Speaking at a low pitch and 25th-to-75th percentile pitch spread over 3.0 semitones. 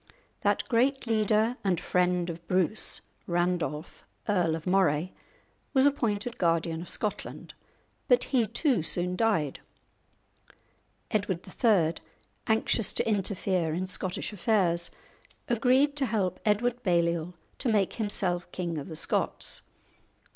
No: high, 190 Hz; average, 4.6 semitones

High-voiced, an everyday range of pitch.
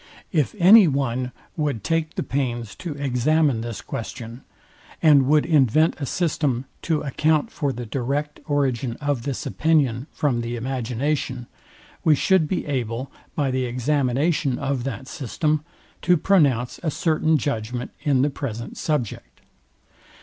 No: medium, 140 Hz; average, 3.8 semitones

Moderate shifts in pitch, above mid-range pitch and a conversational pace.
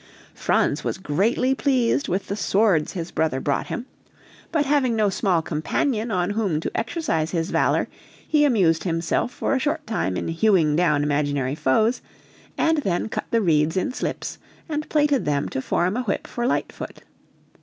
No: wide, 7.4 semitones; high, 195 Hz; average, 170 wpm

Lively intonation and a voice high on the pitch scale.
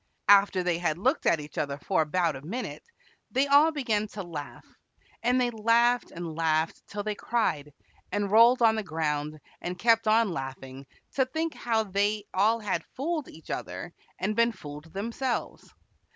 Yes: wide, 6.3 semitones; high, 205 Hz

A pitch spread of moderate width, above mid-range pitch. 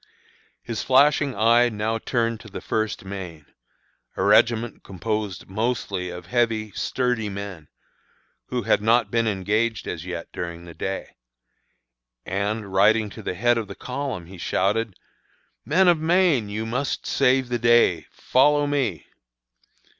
No: average, 3.8 semitones; low, 110 Hz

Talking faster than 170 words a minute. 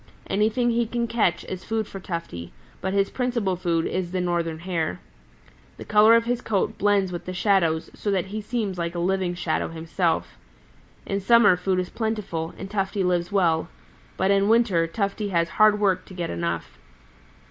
Yes: average, 180 wpm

